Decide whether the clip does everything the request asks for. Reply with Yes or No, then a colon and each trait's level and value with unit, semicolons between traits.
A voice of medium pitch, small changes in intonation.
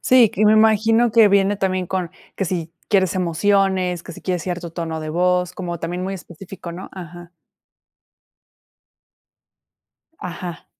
Yes: medium, 180 Hz; narrow, 2.2 semitones